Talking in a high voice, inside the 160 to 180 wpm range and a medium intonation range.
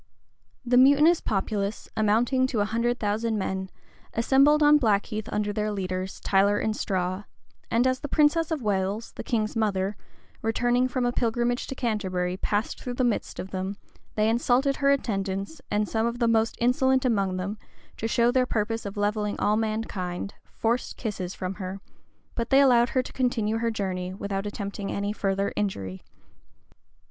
Yes: high, 220 Hz; average, 170 wpm; average, 3.5 semitones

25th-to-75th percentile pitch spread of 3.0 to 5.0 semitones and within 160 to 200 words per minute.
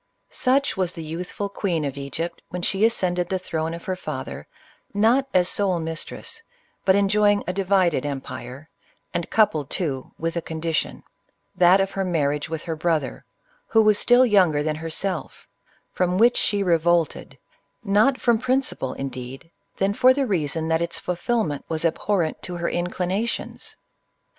Yes: average, 4.0 semitones; average, 165 wpm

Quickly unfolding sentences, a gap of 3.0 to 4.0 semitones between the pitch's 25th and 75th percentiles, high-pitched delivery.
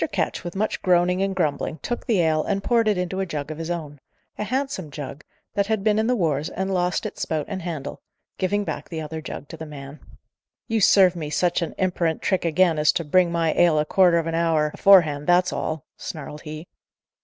No: fast, 225 wpm; average, 3.6 semitones; medium, 170 Hz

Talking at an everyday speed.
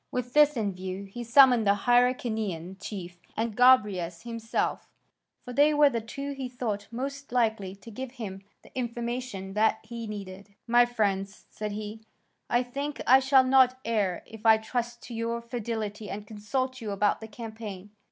Yes: average, 170 wpm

